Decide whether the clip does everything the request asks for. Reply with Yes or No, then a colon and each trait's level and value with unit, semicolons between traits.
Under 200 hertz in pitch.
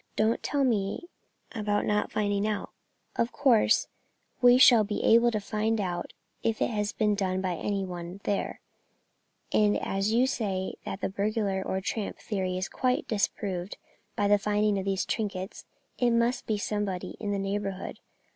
No: high, 205 Hz